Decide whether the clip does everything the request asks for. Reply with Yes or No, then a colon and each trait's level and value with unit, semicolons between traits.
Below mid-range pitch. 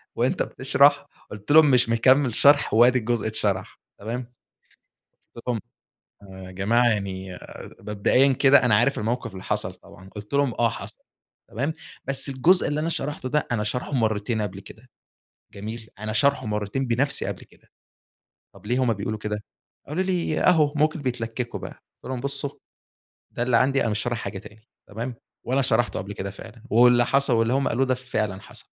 Yes: low, 120 Hz